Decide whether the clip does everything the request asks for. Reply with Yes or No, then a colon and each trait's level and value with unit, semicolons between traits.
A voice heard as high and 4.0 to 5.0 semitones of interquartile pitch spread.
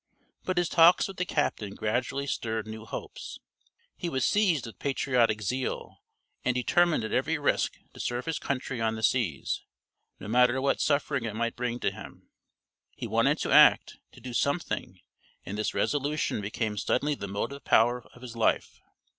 No: low, 125 Hz; average, 4.3 semitones